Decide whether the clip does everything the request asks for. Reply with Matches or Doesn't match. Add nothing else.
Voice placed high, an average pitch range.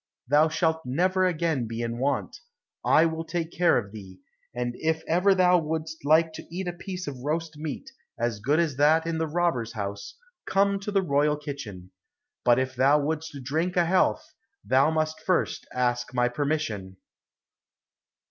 Doesn't match